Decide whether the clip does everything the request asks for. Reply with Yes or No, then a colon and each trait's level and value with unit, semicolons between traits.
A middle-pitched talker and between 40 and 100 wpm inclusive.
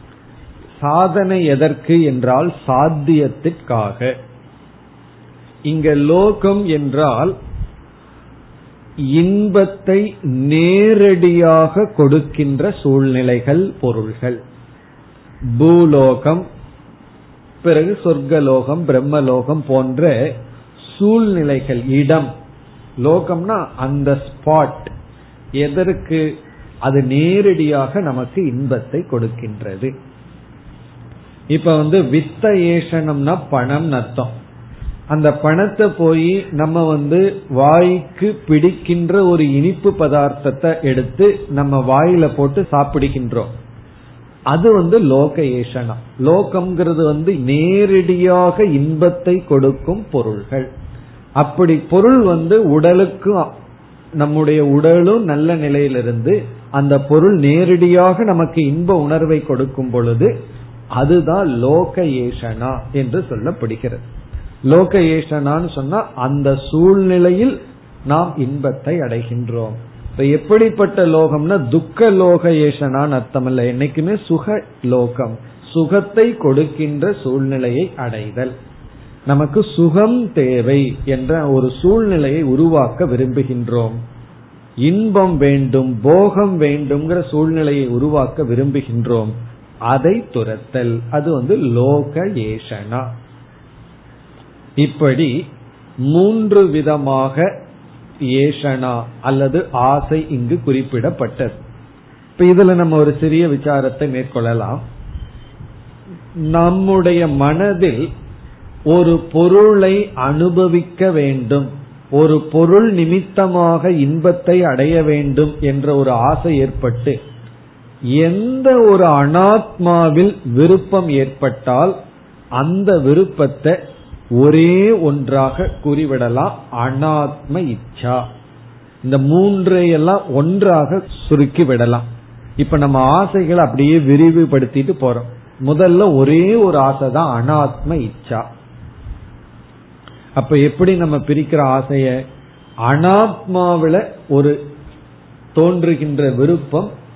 Yes: medium, 145 Hz; slow, 75 wpm